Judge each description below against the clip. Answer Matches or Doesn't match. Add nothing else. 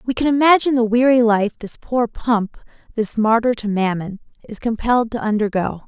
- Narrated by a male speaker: Doesn't match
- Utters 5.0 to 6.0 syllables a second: Matches